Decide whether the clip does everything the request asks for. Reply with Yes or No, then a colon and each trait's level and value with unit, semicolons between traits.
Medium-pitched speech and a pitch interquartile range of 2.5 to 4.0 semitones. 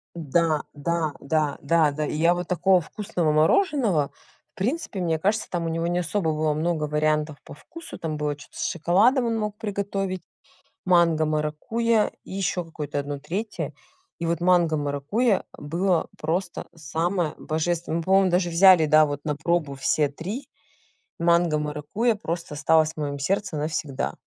Yes: medium, 165 Hz; average, 3.7 semitones